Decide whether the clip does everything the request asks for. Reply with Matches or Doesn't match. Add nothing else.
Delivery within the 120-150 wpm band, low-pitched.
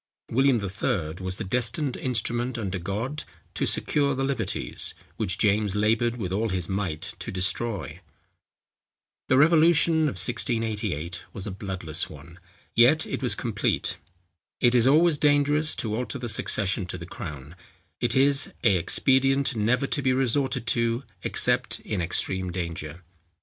Matches